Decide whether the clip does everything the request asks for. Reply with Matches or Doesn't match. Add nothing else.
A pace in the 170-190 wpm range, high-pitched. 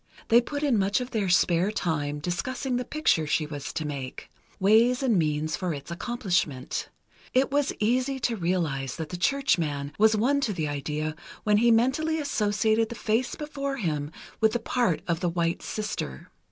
Matches